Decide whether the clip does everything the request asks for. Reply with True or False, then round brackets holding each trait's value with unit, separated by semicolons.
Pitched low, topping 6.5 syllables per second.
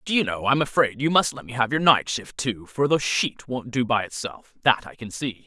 False (125 Hz; 5.4 syllables/s)